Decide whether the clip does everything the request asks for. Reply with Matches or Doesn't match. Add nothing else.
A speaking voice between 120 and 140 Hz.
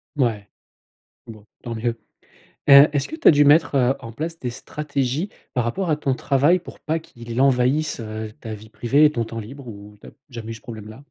Matches